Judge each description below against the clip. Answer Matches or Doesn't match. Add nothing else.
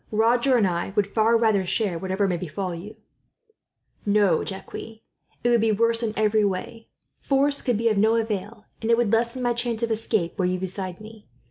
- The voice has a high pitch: Matches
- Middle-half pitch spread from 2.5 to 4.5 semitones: Matches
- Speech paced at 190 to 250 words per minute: Matches